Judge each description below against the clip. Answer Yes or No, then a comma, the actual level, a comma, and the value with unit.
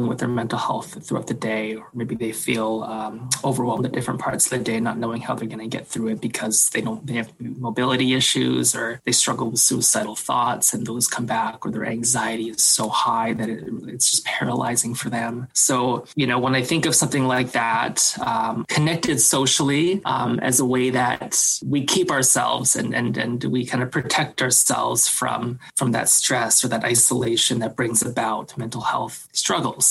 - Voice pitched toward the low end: Yes, low, 120 Hz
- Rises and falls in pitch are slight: Yes, narrow, 2.1 semitones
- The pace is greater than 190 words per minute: Yes, average, 200 wpm